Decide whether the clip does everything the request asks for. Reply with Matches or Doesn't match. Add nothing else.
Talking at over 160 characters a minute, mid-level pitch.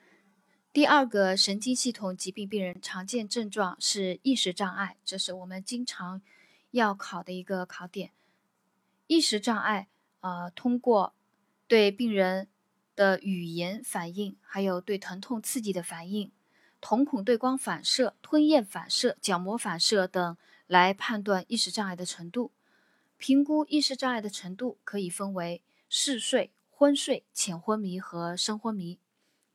Doesn't match